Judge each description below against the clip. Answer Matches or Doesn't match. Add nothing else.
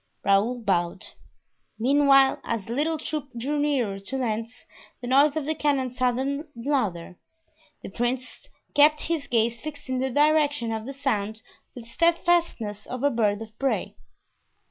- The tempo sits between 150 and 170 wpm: Matches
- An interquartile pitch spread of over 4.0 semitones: Matches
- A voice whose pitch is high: Matches